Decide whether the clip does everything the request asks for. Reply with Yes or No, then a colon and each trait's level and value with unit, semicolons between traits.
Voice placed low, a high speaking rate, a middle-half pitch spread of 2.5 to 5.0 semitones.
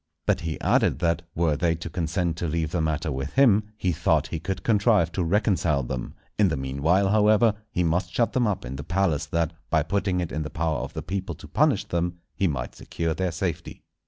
Yes: very low, 85 Hz; fast, 220 wpm; average, 3.5 semitones